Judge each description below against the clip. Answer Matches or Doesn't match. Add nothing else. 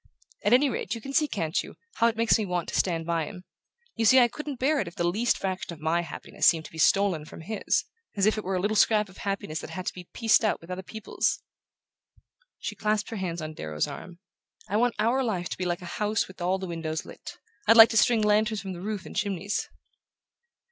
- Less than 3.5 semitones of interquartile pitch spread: Doesn't match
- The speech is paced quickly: Matches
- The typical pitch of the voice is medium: Doesn't match